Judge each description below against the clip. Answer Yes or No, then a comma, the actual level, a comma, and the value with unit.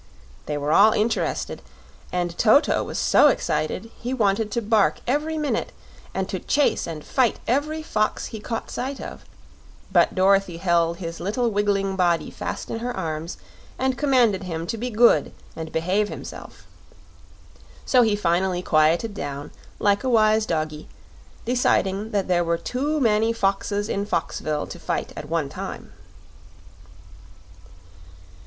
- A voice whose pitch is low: No, high, 205 Hz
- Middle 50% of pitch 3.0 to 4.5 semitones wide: No, wide, 5.4 semitones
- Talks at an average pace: Yes, average, 145 wpm